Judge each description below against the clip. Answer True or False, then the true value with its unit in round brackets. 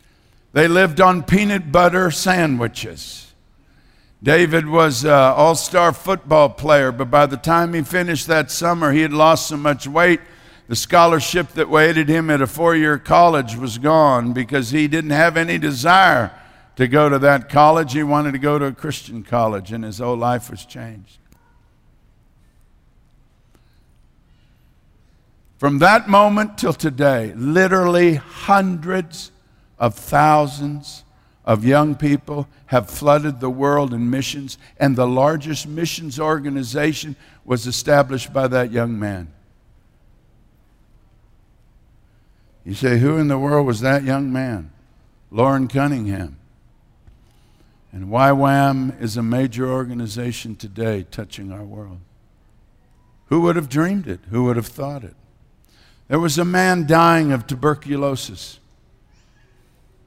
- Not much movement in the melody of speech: False (4.7 semitones)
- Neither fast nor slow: False (130 wpm)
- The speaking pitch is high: False (140 Hz)